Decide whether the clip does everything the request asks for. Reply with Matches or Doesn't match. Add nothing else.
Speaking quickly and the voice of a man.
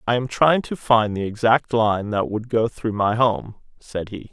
Matches